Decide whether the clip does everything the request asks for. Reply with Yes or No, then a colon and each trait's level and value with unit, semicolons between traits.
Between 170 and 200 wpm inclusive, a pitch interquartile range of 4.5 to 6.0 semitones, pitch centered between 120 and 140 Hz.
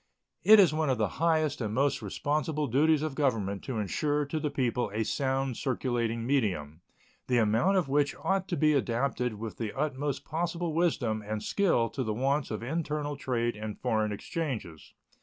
Yes: average, 175 wpm; average, 5.2 semitones; low, 135 Hz